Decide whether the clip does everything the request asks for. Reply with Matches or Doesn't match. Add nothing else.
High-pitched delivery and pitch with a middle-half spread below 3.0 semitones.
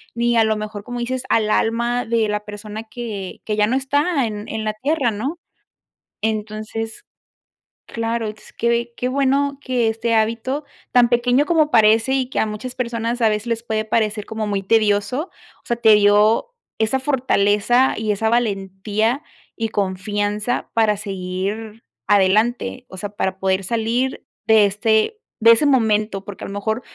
Matches